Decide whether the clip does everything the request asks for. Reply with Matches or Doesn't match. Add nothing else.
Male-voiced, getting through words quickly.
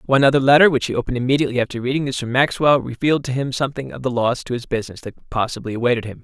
Matches